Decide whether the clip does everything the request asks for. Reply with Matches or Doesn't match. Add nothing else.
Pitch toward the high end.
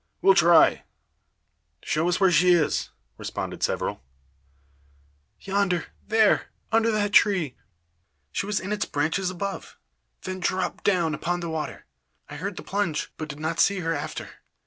Doesn't match